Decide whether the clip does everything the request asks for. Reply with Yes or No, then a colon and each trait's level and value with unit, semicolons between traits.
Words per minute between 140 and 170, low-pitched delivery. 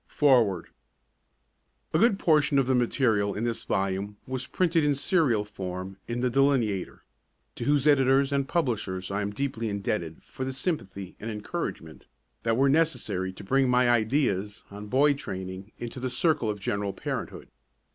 Yes: average, 160 wpm; low, 120 Hz